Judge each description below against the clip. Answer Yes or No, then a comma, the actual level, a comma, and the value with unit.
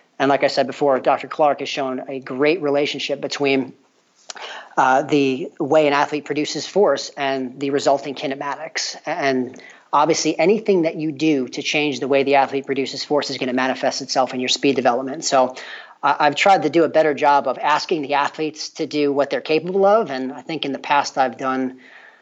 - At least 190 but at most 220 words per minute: Yes, average, 200 wpm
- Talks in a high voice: No, medium, 140 Hz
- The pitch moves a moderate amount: No, narrow, 1.9 semitones